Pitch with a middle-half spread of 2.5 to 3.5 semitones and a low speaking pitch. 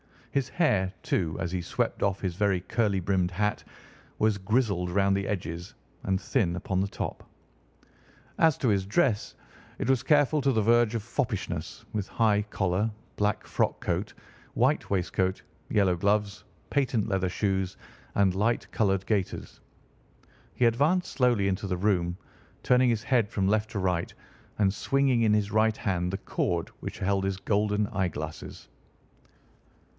Yes: average, 3.0 semitones; low, 100 Hz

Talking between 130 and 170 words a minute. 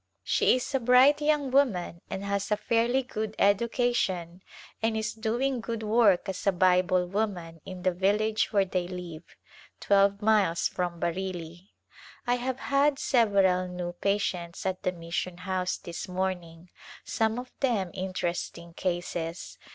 Yes: average, 145 wpm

